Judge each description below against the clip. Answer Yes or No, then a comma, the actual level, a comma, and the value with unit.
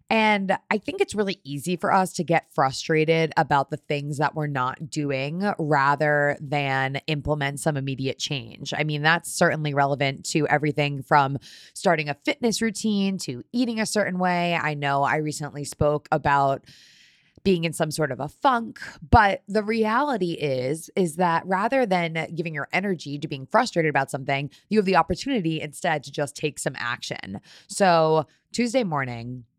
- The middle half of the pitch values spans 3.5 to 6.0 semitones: Yes, average, 4.7 semitones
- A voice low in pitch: No, medium, 155 Hz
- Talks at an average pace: Yes, average, 170 wpm